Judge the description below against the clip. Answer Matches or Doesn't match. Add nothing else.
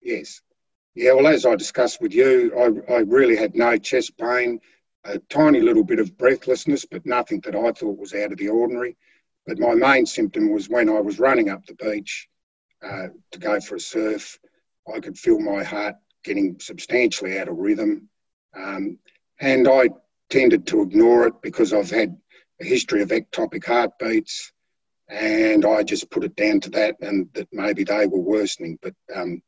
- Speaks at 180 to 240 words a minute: Matches